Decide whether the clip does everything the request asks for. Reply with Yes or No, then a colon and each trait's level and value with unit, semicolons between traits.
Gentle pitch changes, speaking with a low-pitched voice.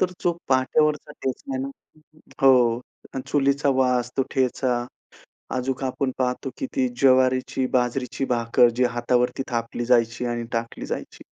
Yes: narrow, 1.9 semitones; low, 130 Hz